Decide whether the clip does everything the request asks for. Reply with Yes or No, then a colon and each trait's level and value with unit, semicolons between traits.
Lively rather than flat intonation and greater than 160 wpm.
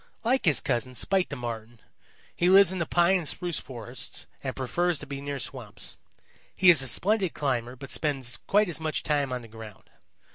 Yes: wide, 5.9 semitones; average, 195 wpm